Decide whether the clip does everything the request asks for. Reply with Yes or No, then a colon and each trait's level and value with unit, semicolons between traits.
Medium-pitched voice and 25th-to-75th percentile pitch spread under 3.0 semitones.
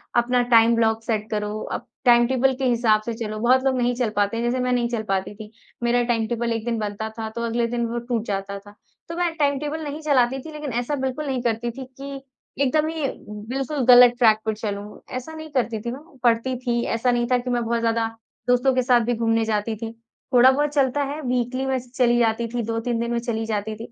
No: high, 240 Hz; narrow, 2.5 semitones